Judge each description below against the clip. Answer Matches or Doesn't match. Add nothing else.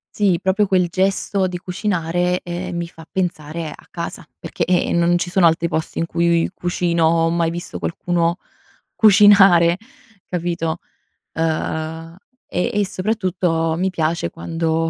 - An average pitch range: Doesn't match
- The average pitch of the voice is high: Doesn't match